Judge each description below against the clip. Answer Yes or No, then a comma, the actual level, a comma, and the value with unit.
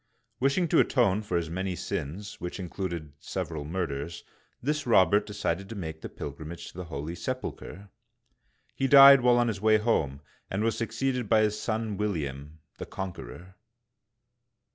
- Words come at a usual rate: Yes, average, 165 wpm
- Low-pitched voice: Yes, very low, 95 Hz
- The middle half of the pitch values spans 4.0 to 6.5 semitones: Yes, average, 5.1 semitones